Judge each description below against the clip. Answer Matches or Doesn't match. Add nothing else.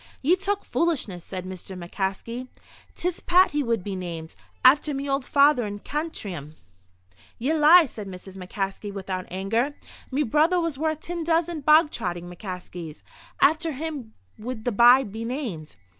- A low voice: Doesn't match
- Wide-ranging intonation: Matches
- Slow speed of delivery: Doesn't match